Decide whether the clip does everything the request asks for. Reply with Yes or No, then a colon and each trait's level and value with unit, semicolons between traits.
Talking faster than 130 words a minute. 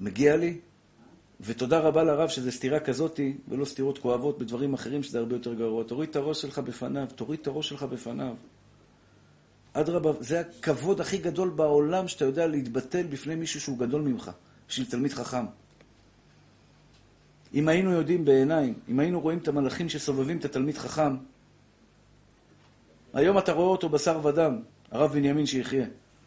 Yes: fast, 150 wpm